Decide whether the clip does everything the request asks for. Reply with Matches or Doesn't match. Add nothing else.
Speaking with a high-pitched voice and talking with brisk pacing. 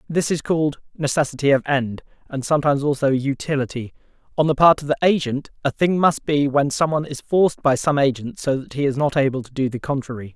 Doesn't match